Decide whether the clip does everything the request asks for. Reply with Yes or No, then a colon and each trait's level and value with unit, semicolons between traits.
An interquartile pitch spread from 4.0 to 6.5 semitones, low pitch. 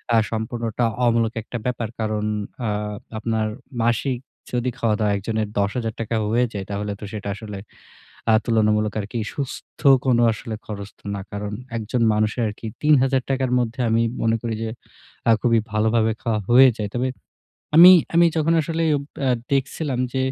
No: average, 2.7 semitones; low, 115 Hz